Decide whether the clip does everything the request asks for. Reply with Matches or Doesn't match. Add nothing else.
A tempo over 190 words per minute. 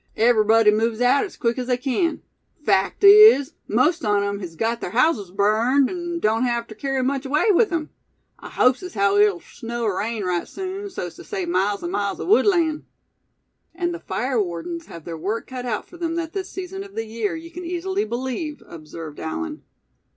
Matches